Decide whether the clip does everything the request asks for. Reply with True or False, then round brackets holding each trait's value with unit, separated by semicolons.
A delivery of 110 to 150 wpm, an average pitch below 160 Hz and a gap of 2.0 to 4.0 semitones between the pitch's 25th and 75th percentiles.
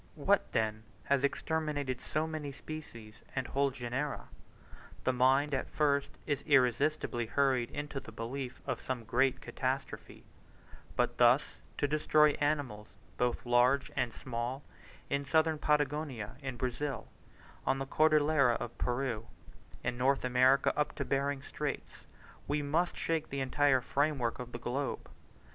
True (140 wpm; 135 Hz; 3.0 semitones)